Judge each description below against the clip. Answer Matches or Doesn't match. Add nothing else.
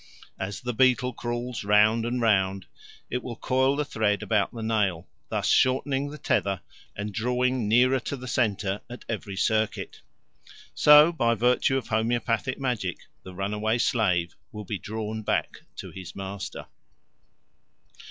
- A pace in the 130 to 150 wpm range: Matches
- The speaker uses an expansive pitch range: Doesn't match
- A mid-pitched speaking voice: Doesn't match